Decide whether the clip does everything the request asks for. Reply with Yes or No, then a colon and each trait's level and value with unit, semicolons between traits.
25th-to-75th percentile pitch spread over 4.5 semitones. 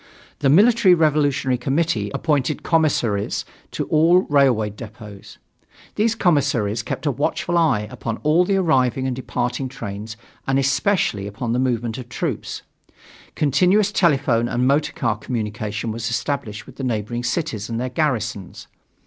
Yes: average, 5.1 semitones